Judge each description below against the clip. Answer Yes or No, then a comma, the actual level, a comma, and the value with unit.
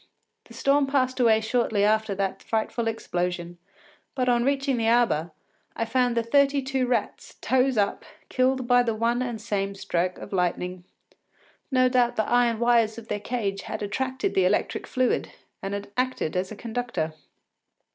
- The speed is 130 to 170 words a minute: Yes, average, 165 wpm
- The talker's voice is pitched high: Yes, high, 230 Hz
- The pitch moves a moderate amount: Yes, average, 3.9 semitones